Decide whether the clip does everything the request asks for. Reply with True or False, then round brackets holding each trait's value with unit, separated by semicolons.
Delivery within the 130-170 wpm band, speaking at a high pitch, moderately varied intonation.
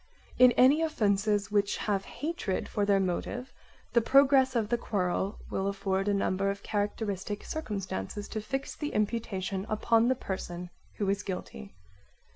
True (150 wpm; 205 Hz; 3.4 semitones)